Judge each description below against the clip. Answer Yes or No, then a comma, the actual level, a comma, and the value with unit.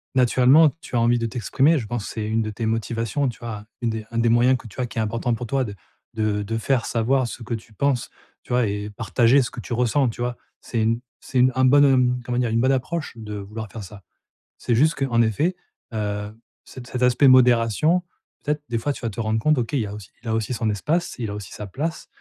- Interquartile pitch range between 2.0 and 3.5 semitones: Yes, average, 2.8 semitones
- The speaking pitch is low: Yes, low, 120 Hz